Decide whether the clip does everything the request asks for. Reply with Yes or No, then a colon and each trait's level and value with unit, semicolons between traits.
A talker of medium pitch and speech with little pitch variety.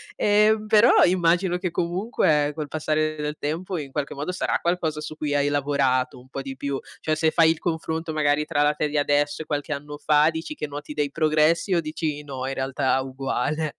Yes: medium, 150 Hz; narrow, 2.2 semitones